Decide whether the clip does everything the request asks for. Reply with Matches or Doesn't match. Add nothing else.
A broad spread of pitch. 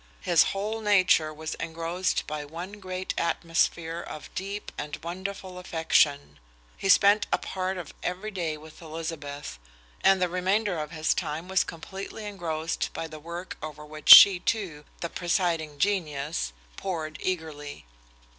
Doesn't match